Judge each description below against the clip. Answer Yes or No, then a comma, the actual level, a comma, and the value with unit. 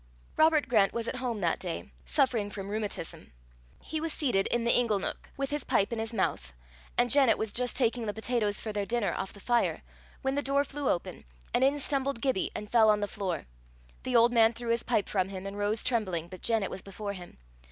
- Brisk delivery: Yes, fast, 225 wpm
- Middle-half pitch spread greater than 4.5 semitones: No, average, 3.8 semitones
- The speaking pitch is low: No, high, 225 Hz